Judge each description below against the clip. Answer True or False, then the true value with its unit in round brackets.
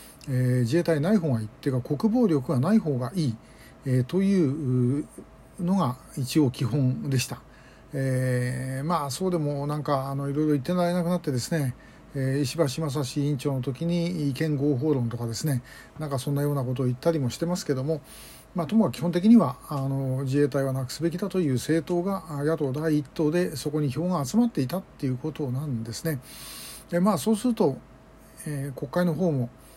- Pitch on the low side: False (145 Hz)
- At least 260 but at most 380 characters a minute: True (365 characters per minute)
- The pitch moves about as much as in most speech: True (4.2 semitones)